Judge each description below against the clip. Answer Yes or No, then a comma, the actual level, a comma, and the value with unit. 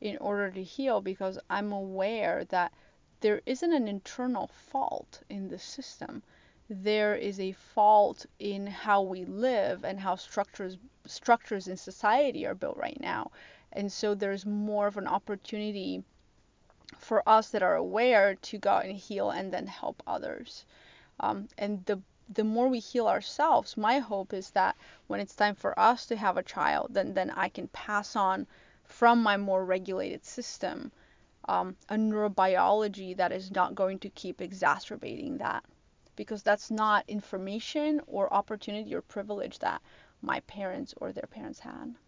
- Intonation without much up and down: Yes, narrow, 2.2 semitones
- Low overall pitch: No, high, 205 Hz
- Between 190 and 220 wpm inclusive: No, average, 160 wpm